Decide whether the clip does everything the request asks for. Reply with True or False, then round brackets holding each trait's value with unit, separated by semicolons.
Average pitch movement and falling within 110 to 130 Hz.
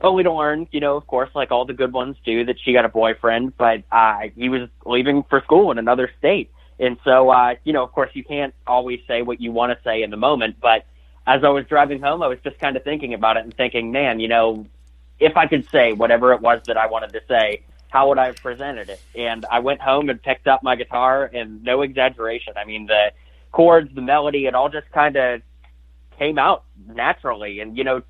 True (3.3 semitones; 125 Hz)